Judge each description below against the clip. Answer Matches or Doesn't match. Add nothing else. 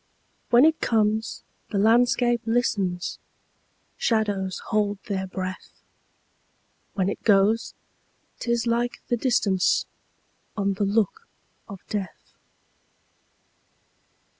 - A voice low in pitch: Doesn't match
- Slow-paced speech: Matches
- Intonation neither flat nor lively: Matches